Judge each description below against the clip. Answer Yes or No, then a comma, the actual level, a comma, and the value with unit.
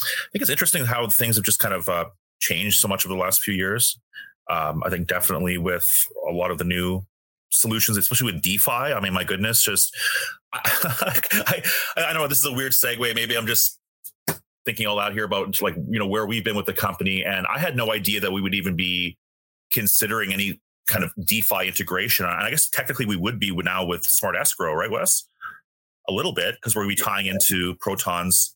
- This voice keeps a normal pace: No, fast, 220 wpm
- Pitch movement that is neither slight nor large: Yes, average, 4.3 semitones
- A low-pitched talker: Yes, low, 105 Hz